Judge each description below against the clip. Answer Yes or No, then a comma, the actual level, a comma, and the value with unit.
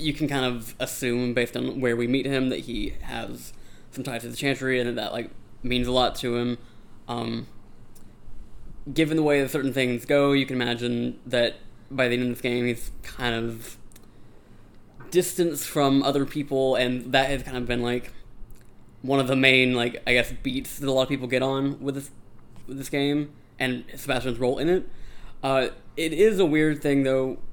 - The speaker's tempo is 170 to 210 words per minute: Yes, average, 200 wpm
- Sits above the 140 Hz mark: No, low, 130 Hz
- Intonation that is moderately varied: No, narrow, 2.2 semitones